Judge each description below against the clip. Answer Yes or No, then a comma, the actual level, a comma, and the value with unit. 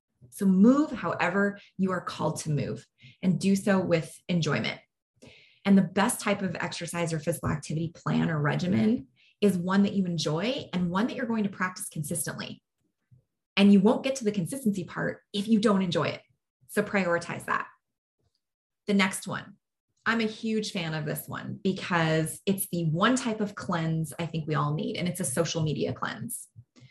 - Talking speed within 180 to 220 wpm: Yes, average, 185 wpm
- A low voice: No, medium, 180 Hz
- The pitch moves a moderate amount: Yes, average, 4.1 semitones